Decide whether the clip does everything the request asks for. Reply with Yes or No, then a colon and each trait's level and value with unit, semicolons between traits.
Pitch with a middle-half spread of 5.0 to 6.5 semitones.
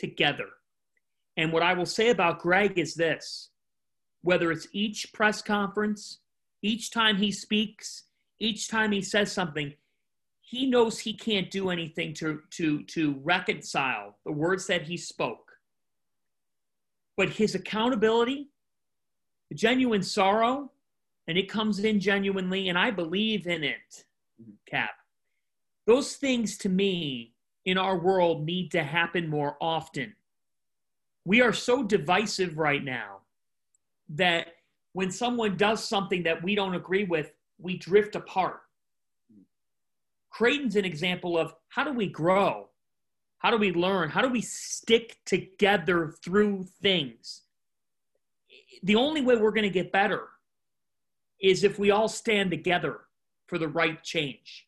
No: average, 4.3 semitones